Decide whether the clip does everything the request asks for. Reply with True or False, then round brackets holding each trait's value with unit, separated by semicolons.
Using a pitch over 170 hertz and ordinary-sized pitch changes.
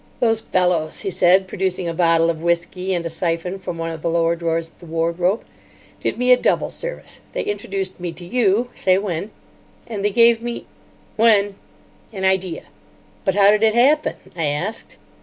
True (185 Hz; 3.7 semitones)